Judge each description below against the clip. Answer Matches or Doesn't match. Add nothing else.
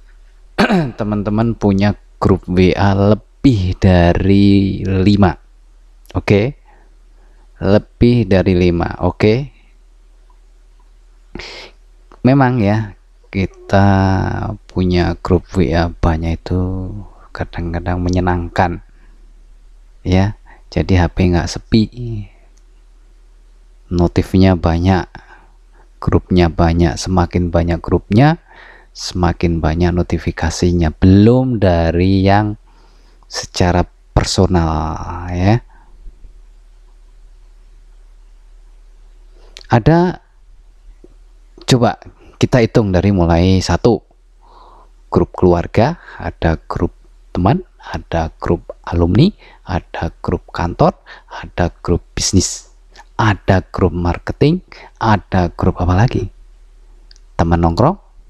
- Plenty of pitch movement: Doesn't match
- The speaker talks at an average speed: Doesn't match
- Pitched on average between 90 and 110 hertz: Matches